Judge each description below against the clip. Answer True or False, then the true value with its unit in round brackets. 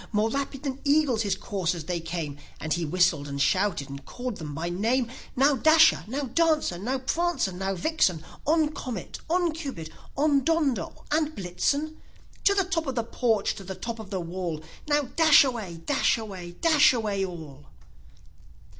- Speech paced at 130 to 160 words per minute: False (170 wpm)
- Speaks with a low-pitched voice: False (225 Hz)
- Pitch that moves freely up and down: True (8.7 semitones)